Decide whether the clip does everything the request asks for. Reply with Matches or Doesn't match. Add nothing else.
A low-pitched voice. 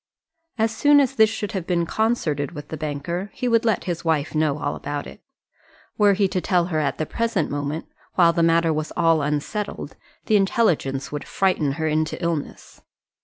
Doesn't match